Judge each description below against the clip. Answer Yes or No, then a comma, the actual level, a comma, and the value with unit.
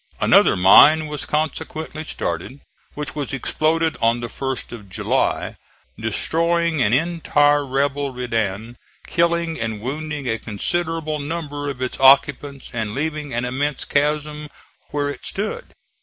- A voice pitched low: No, medium, 145 Hz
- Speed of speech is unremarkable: No, slow, 130 wpm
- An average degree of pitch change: Yes, average, 4.0 semitones